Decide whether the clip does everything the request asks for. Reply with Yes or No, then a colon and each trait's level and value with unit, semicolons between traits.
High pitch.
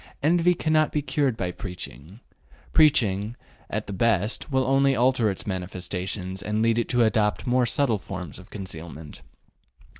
No: low, 110 Hz